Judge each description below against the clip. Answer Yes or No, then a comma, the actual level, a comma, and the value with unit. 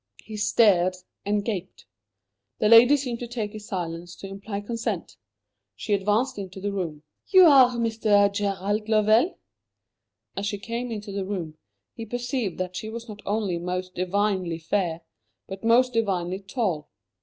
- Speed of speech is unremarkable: Yes, average, 155 wpm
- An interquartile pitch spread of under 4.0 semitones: Yes, average, 3.5 semitones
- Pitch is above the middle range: Yes, high, 205 Hz